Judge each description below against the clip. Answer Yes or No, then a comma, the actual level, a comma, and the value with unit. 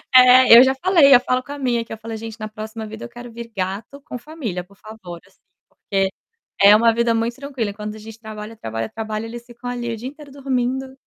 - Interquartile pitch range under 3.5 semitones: Yes, average, 2.9 semitones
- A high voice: Yes, high, 230 Hz